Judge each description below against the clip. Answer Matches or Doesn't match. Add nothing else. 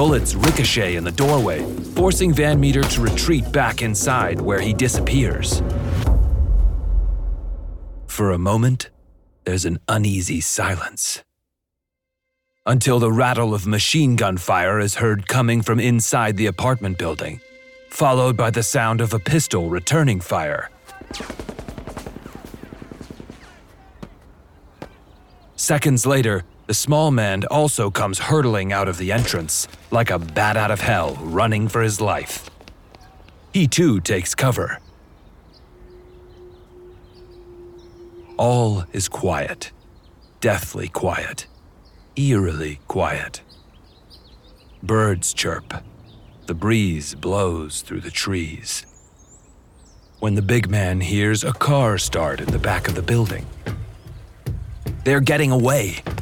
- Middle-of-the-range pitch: Doesn't match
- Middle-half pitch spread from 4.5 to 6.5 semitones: Matches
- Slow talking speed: Matches